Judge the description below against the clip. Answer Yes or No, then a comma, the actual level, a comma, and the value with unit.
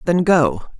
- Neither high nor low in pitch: Yes, medium, 175 Hz